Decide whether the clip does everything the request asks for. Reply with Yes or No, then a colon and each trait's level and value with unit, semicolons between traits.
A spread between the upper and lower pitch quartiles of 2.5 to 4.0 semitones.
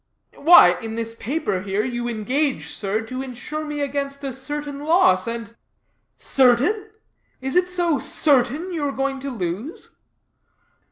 No: average, 4.4 semitones